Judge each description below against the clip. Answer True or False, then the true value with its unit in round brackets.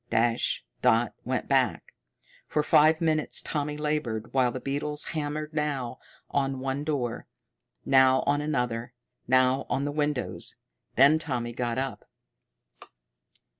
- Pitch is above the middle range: False (135 Hz)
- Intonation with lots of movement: False (3.2 semitones)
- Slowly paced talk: True (125 wpm)